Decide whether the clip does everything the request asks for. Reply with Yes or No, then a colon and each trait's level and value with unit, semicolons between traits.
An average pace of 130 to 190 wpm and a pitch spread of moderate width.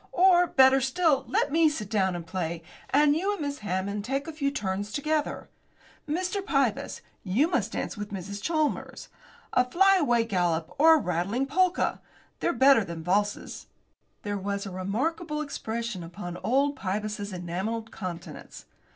No: average, 150 wpm; wide, 7.6 semitones